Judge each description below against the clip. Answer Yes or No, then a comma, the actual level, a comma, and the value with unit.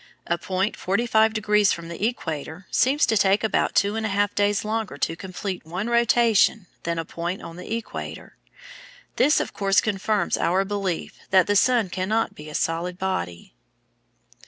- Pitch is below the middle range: No, high, 200 Hz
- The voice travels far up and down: No, average, 3.6 semitones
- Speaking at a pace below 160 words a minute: No, average, 175 wpm